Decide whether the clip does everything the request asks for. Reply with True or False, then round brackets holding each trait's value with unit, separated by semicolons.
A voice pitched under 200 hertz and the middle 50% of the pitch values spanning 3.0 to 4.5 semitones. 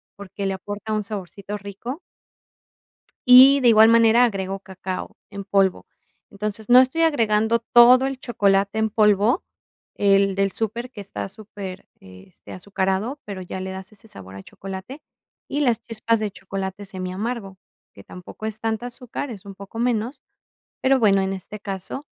False (205 Hz; 3.3 semitones)